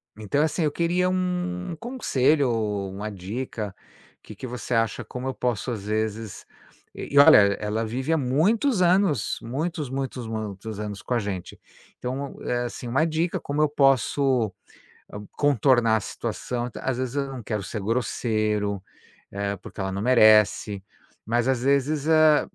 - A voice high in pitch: No, low, 125 Hz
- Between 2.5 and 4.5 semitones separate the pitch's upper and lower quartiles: No, average, 5.2 semitones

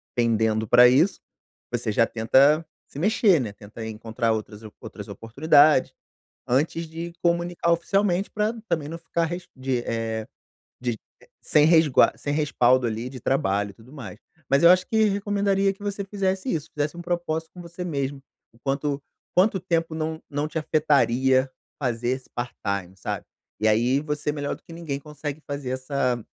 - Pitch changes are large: Yes, wide, 5.8 semitones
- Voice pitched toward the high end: No, medium, 145 Hz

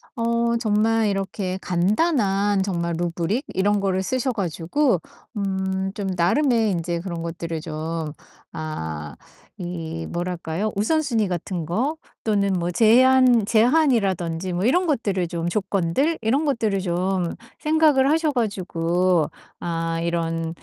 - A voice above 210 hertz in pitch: No, high, 190 Hz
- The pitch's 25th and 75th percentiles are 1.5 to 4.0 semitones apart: No, average, 5.2 semitones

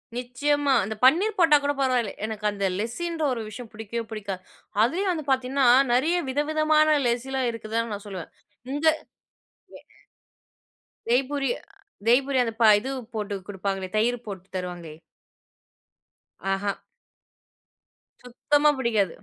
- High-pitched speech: Yes, high, 245 Hz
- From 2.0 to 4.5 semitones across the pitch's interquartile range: No, average, 5.3 semitones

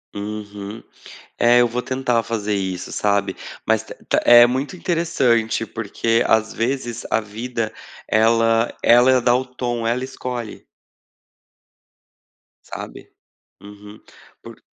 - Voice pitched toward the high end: No, low, 115 Hz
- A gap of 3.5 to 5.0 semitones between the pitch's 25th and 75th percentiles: No, narrow, 2.4 semitones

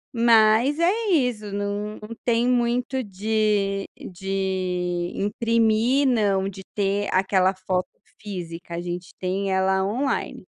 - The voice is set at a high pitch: Yes, high, 205 Hz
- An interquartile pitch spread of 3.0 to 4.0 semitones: Yes, average, 3.4 semitones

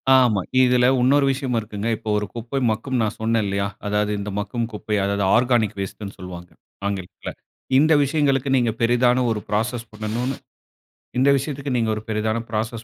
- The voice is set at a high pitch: No, low, 115 Hz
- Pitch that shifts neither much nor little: Yes, average, 3.2 semitones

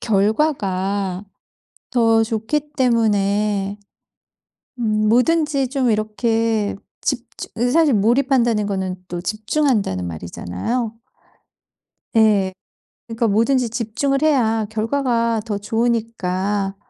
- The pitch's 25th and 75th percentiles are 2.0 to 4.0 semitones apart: Yes, average, 3.3 semitones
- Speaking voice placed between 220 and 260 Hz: Yes, high, 225 Hz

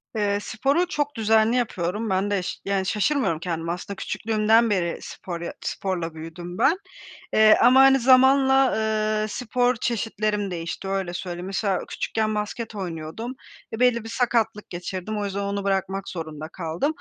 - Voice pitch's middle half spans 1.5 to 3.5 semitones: No, average, 4.0 semitones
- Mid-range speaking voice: No, high, 210 Hz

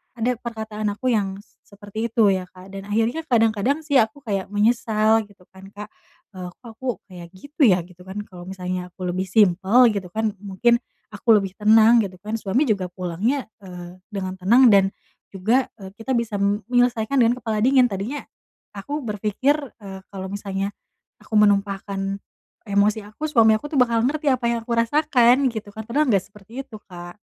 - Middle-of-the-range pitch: No, high, 215 Hz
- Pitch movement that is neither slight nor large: Yes, average, 3.5 semitones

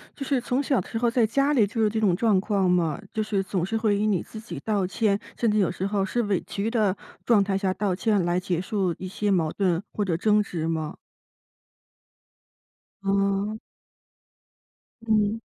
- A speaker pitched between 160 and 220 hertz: Yes, high, 205 Hz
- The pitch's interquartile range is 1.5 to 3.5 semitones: Yes, average, 2.8 semitones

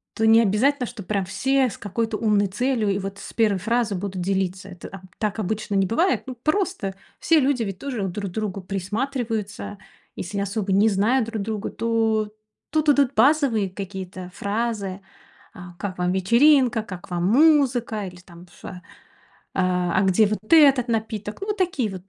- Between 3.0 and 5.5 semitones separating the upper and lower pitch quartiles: Yes, average, 4.1 semitones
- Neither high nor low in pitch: No, high, 215 Hz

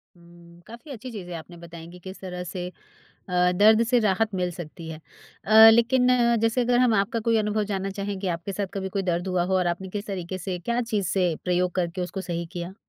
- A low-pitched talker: No, high, 190 Hz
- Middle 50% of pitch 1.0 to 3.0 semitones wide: No, average, 3.4 semitones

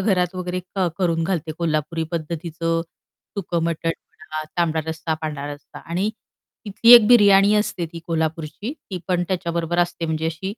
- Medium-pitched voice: Yes, medium, 170 Hz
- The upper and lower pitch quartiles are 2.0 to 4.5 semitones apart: Yes, narrow, 2.6 semitones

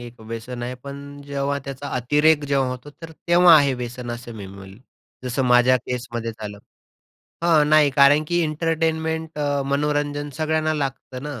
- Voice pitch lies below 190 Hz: Yes, medium, 140 Hz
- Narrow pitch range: No, average, 3.5 semitones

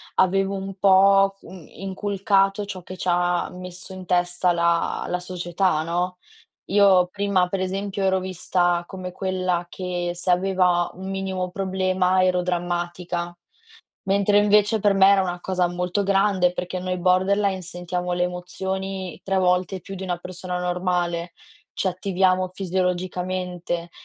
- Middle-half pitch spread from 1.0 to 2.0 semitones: Yes, narrow, 1.4 semitones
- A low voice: No, medium, 185 Hz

